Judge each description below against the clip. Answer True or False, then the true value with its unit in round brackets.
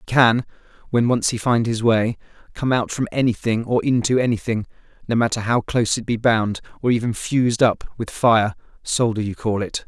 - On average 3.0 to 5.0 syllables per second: False (5.4 syllables/s)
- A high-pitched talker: False (115 Hz)